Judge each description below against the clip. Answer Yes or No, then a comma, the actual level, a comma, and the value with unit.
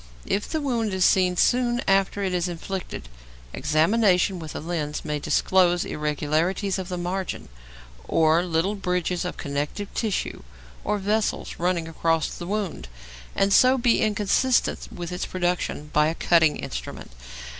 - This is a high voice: No, medium, 180 Hz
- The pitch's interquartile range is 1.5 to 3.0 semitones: No, average, 3.6 semitones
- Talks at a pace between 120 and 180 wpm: Yes, average, 145 wpm